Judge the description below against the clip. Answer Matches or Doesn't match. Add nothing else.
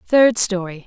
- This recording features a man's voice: Doesn't match